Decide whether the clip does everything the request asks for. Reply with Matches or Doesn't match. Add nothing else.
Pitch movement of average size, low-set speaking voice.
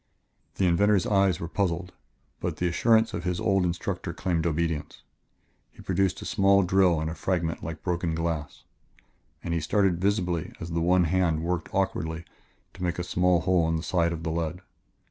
Doesn't match